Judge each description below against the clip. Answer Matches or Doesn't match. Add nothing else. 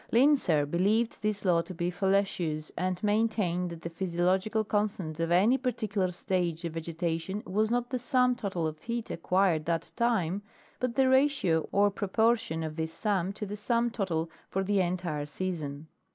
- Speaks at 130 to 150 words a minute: Doesn't match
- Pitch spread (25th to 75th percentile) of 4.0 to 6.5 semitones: Matches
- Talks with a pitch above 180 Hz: Matches